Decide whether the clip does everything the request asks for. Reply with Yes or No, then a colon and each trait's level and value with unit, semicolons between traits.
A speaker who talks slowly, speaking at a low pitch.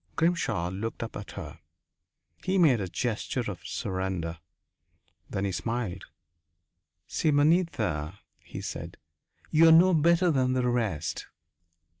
Yes: slow, 120 wpm; low, 120 Hz